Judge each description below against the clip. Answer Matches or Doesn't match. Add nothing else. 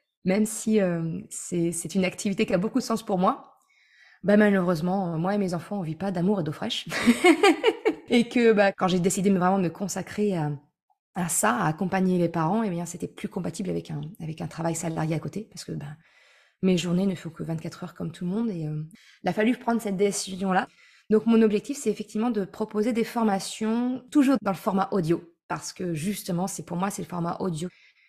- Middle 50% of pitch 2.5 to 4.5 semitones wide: Matches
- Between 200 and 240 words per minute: Matches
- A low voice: Doesn't match